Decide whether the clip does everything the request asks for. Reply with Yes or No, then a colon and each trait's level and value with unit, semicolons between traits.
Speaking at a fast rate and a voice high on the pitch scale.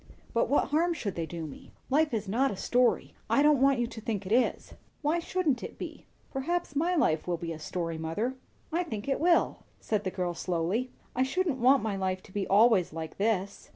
Yes: fast, 220 wpm; high, 230 Hz